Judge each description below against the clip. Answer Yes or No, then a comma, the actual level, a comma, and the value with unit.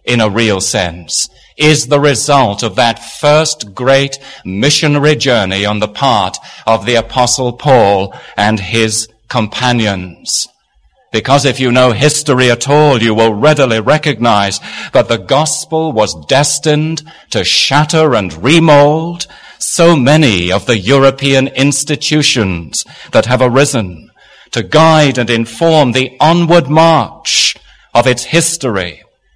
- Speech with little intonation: No, average, 5.0 semitones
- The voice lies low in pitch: Yes, low, 130 Hz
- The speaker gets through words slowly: Yes, slow, 125 wpm